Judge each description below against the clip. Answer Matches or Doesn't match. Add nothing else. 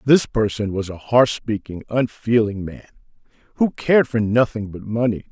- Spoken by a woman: Doesn't match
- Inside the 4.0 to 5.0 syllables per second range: Matches